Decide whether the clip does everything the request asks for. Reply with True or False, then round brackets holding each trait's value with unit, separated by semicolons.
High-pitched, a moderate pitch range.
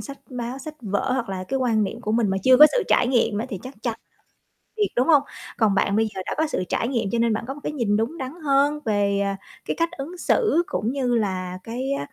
True (240 Hz; 4.6 semitones)